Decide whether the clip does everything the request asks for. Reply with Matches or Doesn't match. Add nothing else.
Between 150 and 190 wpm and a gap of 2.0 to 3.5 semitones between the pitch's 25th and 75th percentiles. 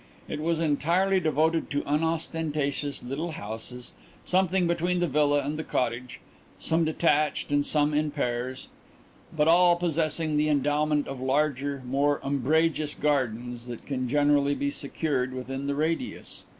Doesn't match